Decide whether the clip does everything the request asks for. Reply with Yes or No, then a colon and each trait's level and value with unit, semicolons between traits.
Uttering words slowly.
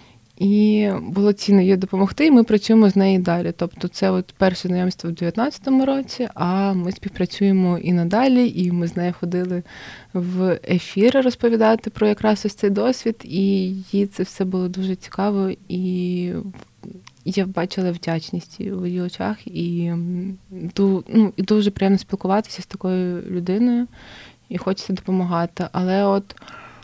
No: average, 150 wpm